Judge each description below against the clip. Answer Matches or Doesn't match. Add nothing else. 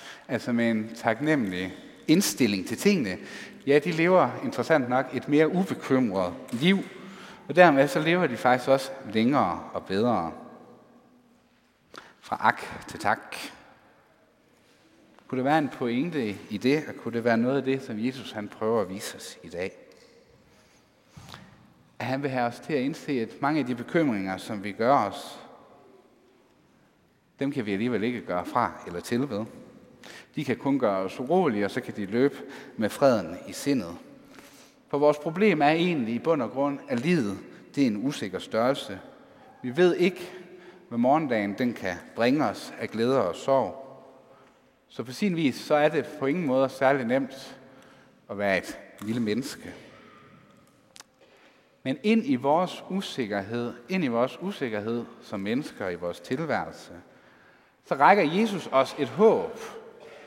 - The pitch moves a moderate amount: Doesn't match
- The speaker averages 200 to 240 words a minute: Doesn't match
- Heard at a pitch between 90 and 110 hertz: Doesn't match